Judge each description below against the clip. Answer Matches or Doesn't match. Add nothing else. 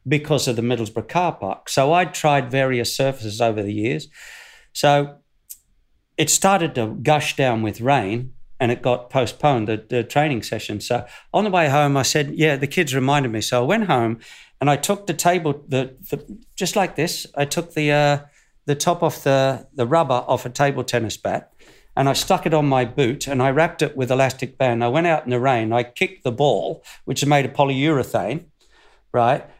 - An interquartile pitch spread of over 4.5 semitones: Doesn't match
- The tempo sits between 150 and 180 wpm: Doesn't match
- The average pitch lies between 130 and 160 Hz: Matches